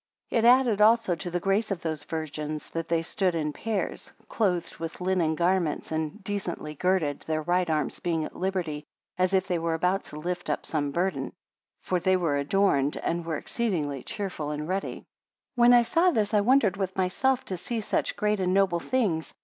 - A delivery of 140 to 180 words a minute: No, average, 200 wpm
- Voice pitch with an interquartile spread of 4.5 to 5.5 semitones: No, average, 3.9 semitones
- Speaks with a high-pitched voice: No, medium, 180 Hz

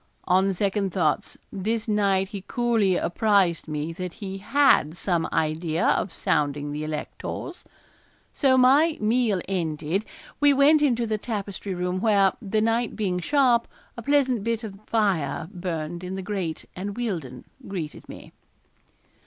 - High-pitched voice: Yes, high, 195 Hz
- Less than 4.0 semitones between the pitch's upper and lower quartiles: No, average, 4.8 semitones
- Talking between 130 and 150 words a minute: Yes, average, 145 wpm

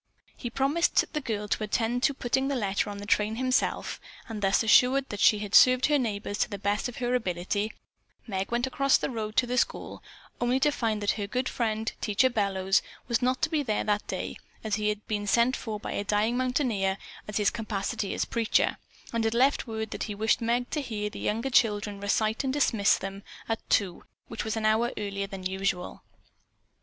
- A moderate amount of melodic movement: Yes, average, 3.3 semitones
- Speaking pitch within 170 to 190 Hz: No, high, 220 Hz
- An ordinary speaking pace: No, fast, 210 wpm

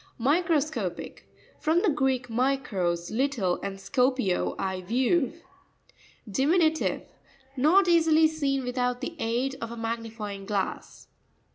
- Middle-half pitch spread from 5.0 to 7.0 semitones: Yes, wide, 5.5 semitones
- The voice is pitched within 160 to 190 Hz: No, very high, 255 Hz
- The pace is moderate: No, slow, 120 wpm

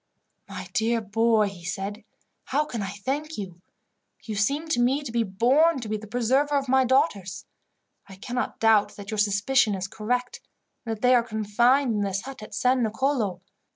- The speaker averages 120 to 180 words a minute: No, average, 190 wpm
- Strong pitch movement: No, average, 4.2 semitones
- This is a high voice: Yes, high, 225 Hz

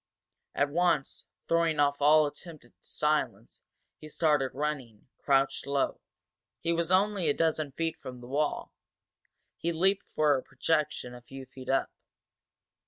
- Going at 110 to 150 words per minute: Yes, average, 145 wpm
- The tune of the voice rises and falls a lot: No, average, 3.3 semitones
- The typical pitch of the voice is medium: Yes, medium, 150 Hz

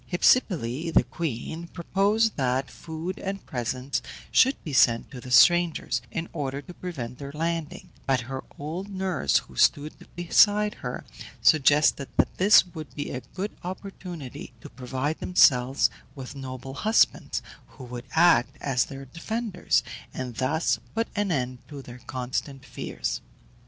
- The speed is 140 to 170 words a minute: Yes, average, 145 wpm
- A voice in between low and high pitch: Yes, medium, 145 Hz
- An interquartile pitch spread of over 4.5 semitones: Yes, wide, 5.4 semitones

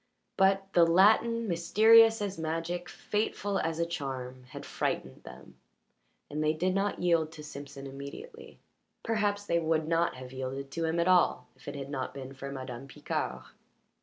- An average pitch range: No, wide, 5.8 semitones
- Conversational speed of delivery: Yes, average, 165 wpm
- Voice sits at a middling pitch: Yes, medium, 165 Hz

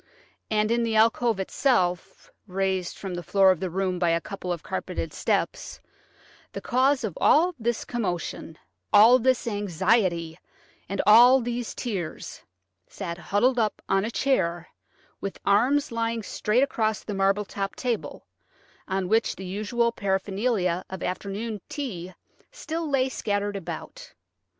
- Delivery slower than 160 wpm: Yes, average, 140 wpm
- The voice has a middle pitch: No, high, 205 Hz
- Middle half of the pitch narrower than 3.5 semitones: No, average, 4.1 semitones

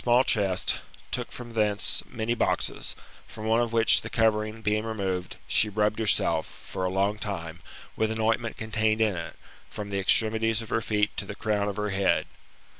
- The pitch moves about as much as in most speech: No, narrow, 1.7 semitones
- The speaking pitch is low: Yes, low, 110 Hz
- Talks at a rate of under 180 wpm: No, average, 195 wpm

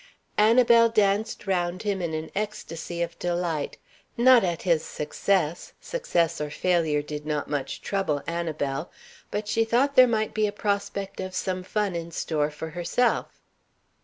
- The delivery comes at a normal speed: Yes, average, 155 wpm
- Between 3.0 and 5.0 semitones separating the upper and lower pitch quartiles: Yes, average, 4.7 semitones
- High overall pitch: No, medium, 180 Hz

